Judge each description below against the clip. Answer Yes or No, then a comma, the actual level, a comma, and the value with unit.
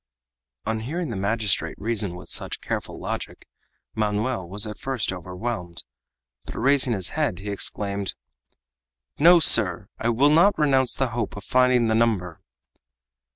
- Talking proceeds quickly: No, average, 145 wpm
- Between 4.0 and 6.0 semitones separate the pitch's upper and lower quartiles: Yes, average, 4.4 semitones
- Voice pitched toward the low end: Yes, low, 110 Hz